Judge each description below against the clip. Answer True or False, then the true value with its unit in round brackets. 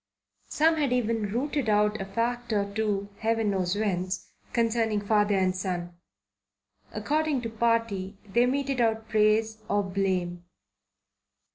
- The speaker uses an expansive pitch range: False (3.0 semitones)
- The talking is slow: True (130 wpm)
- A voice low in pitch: False (215 Hz)